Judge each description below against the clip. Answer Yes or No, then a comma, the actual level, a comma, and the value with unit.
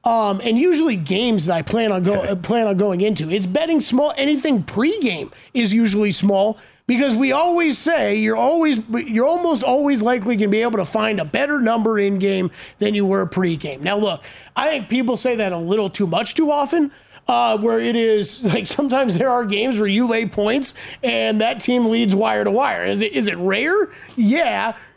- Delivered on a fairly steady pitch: No, average, 4.4 semitones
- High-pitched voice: Yes, high, 225 Hz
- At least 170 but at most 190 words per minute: No, fast, 205 wpm